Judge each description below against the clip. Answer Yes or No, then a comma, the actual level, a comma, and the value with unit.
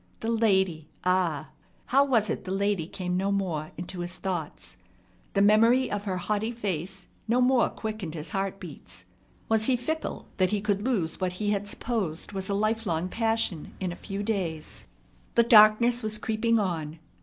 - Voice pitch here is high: Yes, high, 200 Hz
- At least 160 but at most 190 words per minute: Yes, average, 175 wpm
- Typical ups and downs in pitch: Yes, average, 3.7 semitones